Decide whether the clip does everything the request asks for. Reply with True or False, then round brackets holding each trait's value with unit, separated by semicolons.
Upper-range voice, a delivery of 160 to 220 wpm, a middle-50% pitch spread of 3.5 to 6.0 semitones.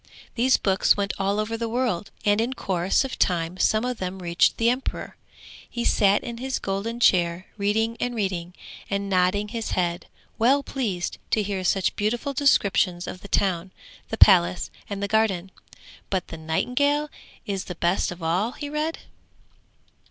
True (200 Hz; 165 wpm; 4.4 semitones)